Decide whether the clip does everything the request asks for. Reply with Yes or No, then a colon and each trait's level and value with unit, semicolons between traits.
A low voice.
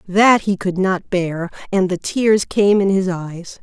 No: high, 190 Hz